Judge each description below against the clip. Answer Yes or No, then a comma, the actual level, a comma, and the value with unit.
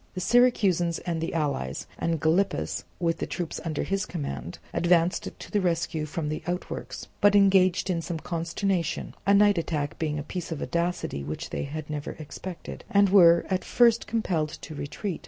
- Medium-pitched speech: Yes, medium, 170 Hz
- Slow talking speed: No, average, 175 wpm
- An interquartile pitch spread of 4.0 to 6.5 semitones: No, average, 3.4 semitones